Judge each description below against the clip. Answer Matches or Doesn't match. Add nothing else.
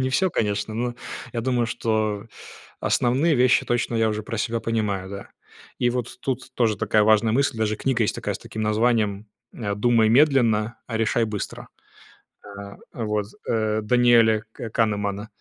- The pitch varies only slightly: Matches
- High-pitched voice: Doesn't match